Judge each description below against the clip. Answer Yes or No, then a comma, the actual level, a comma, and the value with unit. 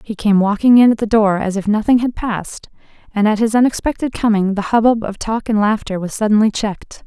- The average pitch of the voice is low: No, high, 215 Hz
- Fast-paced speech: Yes, fast, 220 wpm